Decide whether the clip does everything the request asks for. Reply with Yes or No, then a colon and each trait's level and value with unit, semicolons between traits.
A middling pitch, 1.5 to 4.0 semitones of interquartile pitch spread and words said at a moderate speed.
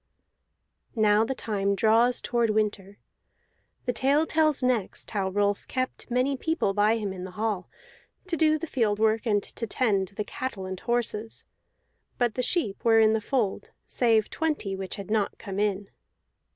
No: high, 220 Hz; average, 3.6 semitones; average, 165 wpm